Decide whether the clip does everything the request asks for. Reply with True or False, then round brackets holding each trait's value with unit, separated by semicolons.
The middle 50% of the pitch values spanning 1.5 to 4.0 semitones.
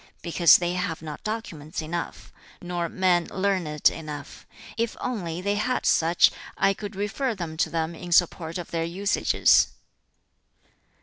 True (3.4 semitones)